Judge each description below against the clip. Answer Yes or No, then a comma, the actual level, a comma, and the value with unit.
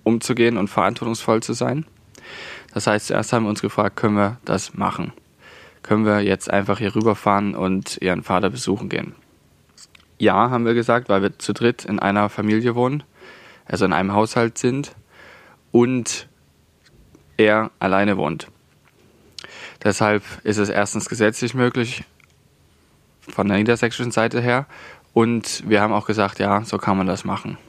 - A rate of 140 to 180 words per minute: Yes, average, 150 wpm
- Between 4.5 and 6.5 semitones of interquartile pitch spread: No, average, 2.7 semitones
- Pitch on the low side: Yes, low, 105 Hz